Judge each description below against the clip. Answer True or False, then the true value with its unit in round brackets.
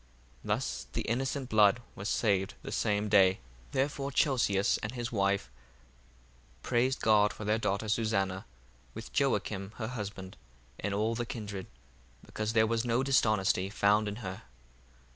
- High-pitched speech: False (105 Hz)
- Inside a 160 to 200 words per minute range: False (145 wpm)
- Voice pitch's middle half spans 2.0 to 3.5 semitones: True (3.0 semitones)